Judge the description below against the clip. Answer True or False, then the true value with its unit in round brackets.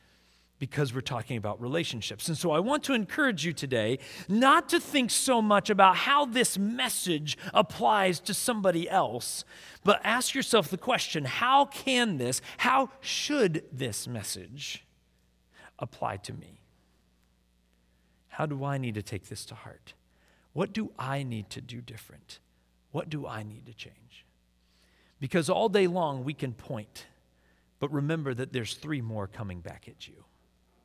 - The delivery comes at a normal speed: True (155 wpm)